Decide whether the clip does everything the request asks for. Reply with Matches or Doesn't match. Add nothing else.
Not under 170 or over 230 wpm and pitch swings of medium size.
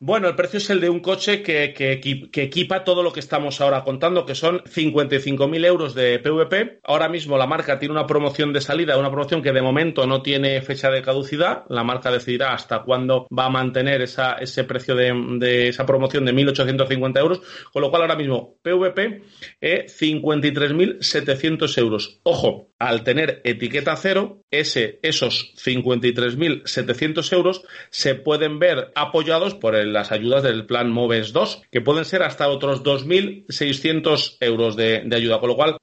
Matches